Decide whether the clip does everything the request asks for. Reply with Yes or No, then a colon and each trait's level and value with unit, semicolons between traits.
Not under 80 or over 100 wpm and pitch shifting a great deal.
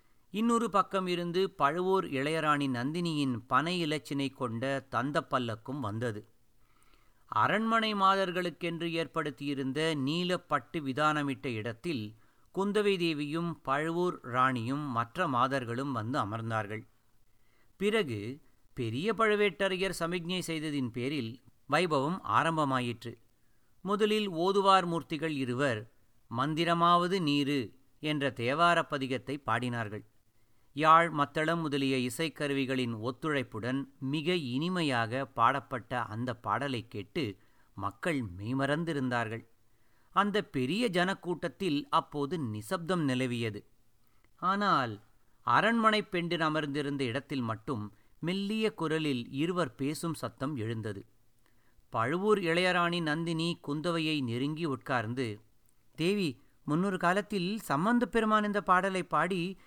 Yes: average, 90 wpm; wide, 6.0 semitones